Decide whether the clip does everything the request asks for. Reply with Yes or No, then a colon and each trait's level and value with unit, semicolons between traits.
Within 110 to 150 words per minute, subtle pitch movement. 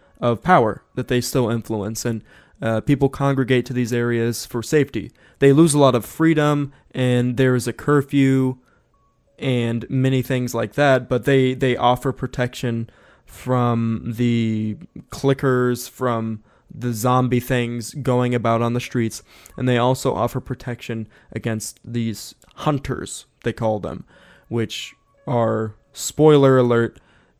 Yes: average, 140 wpm; narrow, 2.3 semitones